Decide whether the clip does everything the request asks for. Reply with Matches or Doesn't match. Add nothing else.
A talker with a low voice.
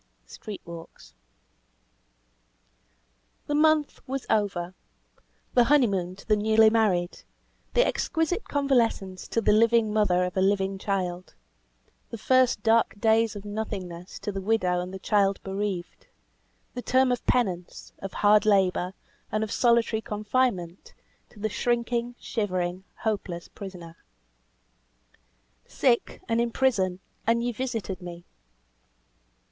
Doesn't match